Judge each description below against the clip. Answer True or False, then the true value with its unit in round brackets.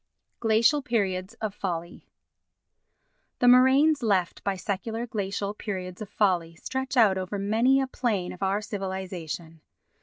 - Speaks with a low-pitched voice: False (205 Hz)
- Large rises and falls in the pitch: False (4.0 semitones)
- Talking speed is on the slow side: True (130 wpm)